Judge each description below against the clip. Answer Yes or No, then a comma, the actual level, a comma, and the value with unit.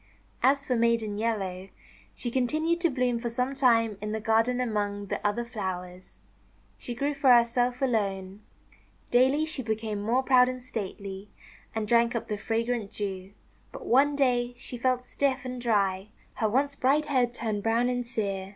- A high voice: Yes, high, 235 Hz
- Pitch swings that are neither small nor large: Yes, average, 3.3 semitones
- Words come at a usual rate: Yes, average, 170 wpm